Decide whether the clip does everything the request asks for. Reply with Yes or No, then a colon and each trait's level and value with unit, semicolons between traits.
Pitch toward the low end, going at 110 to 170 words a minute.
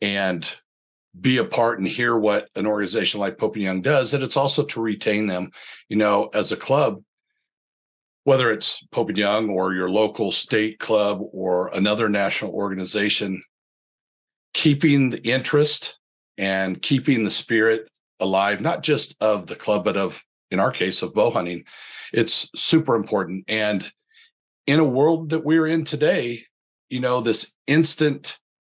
Yes: low, 110 Hz; average, 155 wpm